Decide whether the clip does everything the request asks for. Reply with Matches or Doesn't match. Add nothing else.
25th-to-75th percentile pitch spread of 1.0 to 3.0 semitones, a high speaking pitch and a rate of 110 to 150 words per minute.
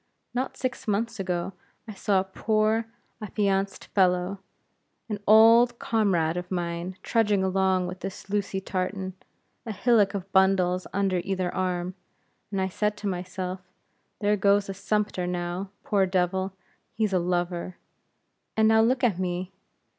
Matches